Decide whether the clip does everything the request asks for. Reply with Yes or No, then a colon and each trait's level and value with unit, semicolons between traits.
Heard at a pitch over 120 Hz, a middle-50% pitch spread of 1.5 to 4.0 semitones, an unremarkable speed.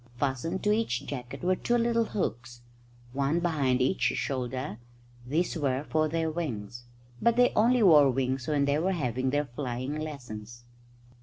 No: medium, 140 Hz; average, 5.2 semitones; average, 155 wpm